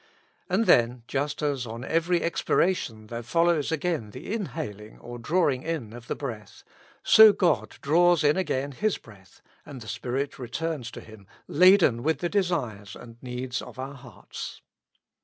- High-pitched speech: No, medium, 140 Hz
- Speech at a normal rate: Yes, average, 160 wpm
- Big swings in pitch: Yes, wide, 6.0 semitones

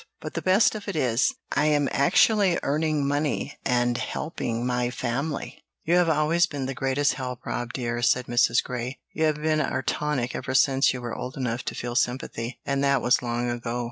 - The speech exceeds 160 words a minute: Yes, average, 200 wpm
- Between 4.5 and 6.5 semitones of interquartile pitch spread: No, average, 3.7 semitones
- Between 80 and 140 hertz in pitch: Yes, low, 135 Hz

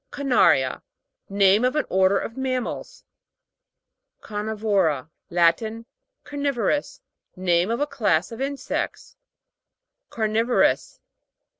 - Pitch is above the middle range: Yes, high, 220 Hz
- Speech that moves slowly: Yes, slow, 90 wpm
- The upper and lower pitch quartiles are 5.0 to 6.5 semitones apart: Yes, wide, 5.4 semitones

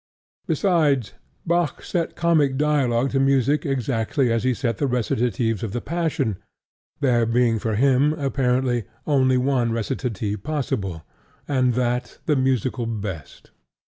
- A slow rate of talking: Yes, slow, 130 wpm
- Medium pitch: No, low, 125 Hz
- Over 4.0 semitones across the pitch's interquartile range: No, average, 3.3 semitones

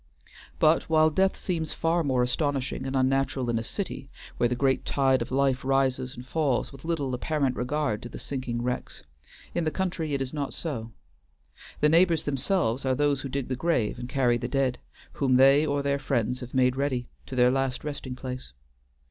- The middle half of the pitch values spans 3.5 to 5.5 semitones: No, average, 2.7 semitones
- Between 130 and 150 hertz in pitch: Yes, low, 135 Hz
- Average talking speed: Yes, average, 195 wpm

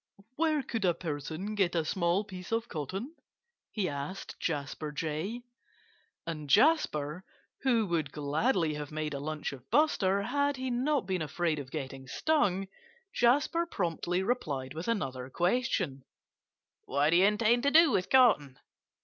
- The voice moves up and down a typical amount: No, wide, 7.8 semitones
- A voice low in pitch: No, medium, 180 Hz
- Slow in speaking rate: No, average, 150 wpm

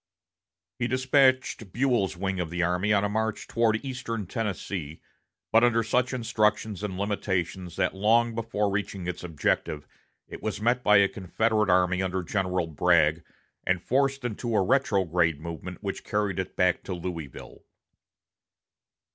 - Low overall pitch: Yes, low, 100 Hz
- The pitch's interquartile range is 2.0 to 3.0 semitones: No, average, 4.0 semitones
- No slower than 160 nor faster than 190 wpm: No, average, 145 wpm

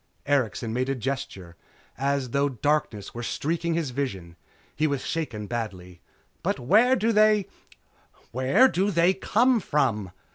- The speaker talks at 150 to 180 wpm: No, average, 140 wpm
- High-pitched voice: No, medium, 140 Hz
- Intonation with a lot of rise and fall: Yes, wide, 6.4 semitones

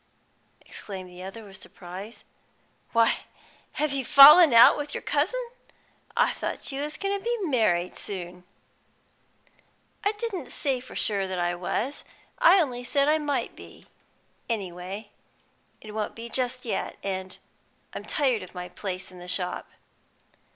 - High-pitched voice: Yes, high, 230 Hz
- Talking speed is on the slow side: No, average, 150 wpm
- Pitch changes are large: Yes, wide, 7.5 semitones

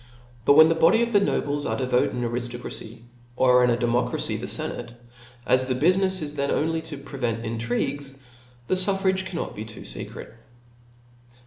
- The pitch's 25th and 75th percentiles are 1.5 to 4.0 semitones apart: No, average, 5.2 semitones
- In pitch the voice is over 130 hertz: Yes, medium, 140 Hz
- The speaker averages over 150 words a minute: Yes, average, 190 wpm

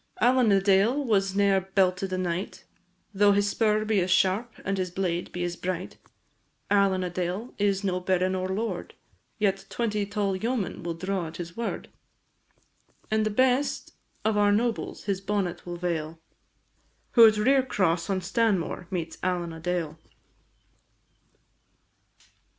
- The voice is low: No, high, 195 Hz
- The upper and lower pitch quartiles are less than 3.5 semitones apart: Yes, average, 2.8 semitones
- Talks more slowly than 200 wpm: Yes, average, 150 wpm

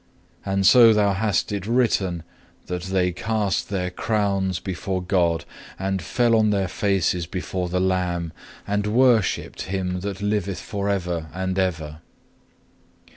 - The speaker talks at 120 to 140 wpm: Yes, slow, 135 wpm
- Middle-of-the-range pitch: No, very low, 95 Hz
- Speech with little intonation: Yes, narrow, 2.2 semitones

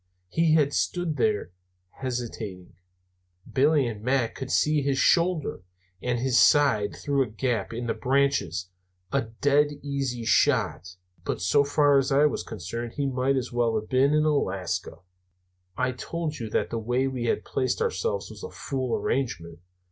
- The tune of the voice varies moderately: Yes, average, 4.0 semitones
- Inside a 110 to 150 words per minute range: No, average, 165 wpm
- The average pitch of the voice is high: No, low, 130 Hz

